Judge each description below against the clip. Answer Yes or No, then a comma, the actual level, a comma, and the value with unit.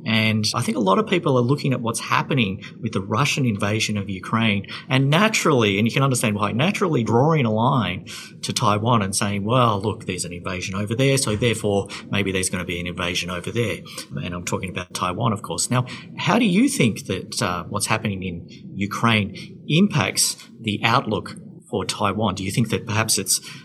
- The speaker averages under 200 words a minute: No, fast, 205 wpm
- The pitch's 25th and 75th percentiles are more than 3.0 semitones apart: Yes, average, 4.1 semitones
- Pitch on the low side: Yes, low, 110 Hz